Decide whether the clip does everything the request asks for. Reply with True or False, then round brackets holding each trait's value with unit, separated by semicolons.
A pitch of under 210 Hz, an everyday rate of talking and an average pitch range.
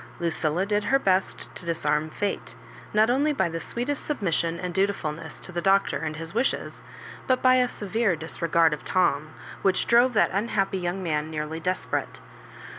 True (185 Hz; 170 wpm; 4.7 semitones)